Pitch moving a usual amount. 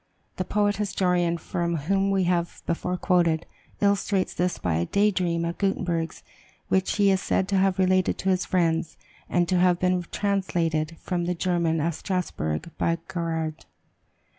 No: narrow, 2.2 semitones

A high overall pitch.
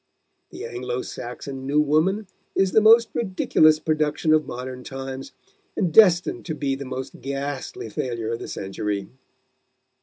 No: medium, 140 Hz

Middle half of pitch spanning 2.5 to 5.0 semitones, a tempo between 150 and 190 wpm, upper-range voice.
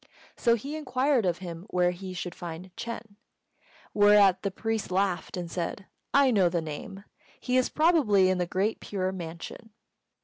Yes: average, 4.2 semitones; average, 165 wpm; high, 195 Hz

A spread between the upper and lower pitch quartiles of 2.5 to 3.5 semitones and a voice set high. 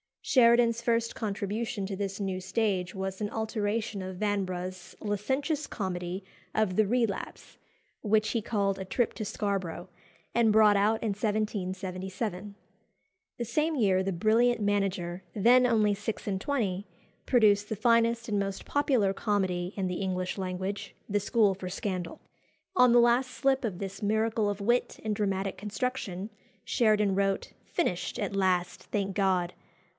Yes: average, 3.0 semitones; high, 205 Hz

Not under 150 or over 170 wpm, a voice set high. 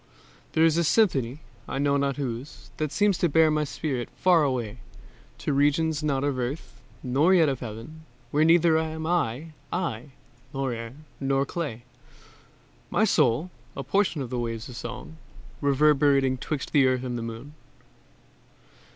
No: average, 155 wpm; medium, 140 Hz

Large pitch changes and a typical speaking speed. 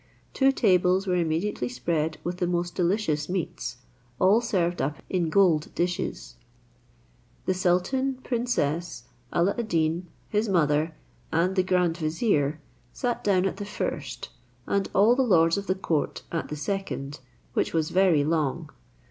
No: average, 3.7 semitones; average, 150 wpm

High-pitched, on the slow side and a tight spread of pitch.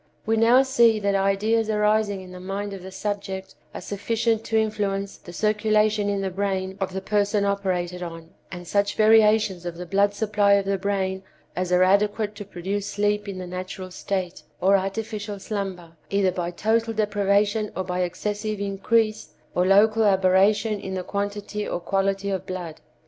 No: high, 200 Hz; average, 175 wpm; narrow, 2.0 semitones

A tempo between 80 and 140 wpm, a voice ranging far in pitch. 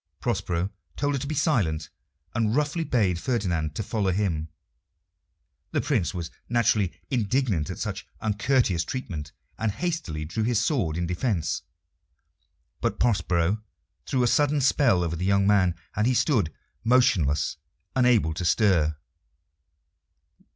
Yes: slow, 135 wpm; wide, 6.5 semitones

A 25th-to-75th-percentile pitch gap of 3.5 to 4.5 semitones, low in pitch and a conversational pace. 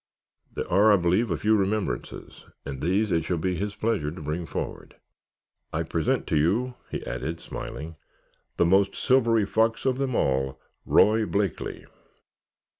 No: average, 5.1 semitones; very low, 95 Hz; average, 155 wpm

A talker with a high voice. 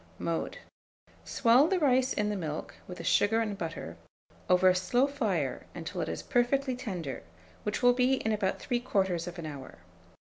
Yes: high, 210 Hz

